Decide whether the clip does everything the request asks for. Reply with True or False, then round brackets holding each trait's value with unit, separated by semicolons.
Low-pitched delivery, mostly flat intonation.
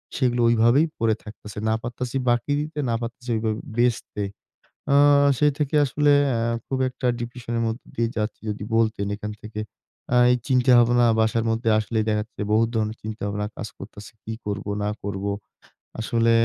True (115 Hz; 2.2 semitones)